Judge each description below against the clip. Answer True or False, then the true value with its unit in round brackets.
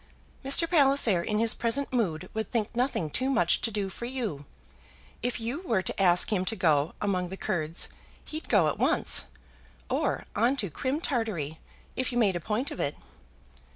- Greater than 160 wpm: True (185 wpm)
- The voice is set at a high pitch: True (220 Hz)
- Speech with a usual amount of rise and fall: False (5.9 semitones)